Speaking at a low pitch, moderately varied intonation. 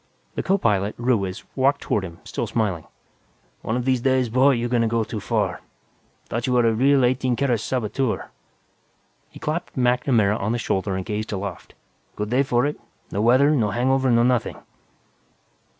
Yes: low, 120 Hz; average, 3.5 semitones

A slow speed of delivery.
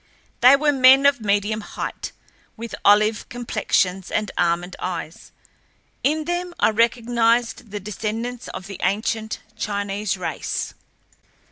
Yes: slow, 120 wpm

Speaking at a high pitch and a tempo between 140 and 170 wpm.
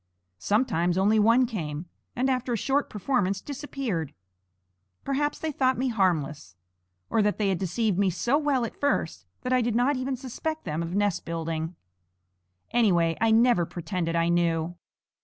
Yes: high, 210 Hz; average, 160 wpm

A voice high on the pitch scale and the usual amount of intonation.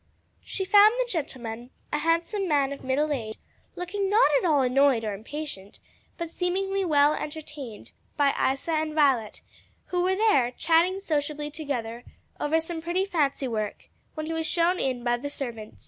Yes: very high, 300 Hz; average, 4.8 semitones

